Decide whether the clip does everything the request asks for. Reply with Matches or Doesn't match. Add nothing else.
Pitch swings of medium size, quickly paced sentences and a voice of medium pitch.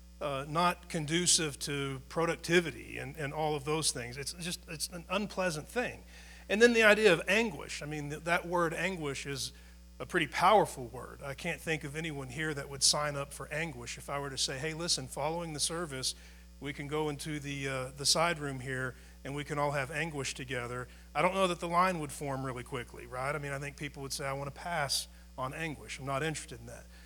Matches